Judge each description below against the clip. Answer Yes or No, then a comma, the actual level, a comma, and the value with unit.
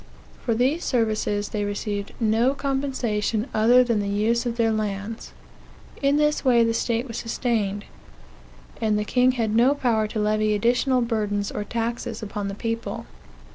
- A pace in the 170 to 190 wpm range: No, average, 160 wpm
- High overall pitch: Yes, high, 225 Hz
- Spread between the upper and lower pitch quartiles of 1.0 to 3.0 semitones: Yes, average, 2.7 semitones